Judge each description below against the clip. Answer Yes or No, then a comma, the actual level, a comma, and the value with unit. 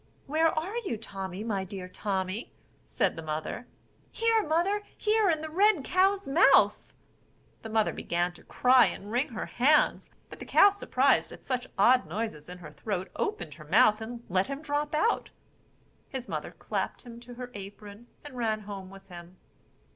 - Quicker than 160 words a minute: Yes, average, 175 wpm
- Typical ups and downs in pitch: No, wide, 7.9 semitones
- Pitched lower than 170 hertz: No, high, 230 Hz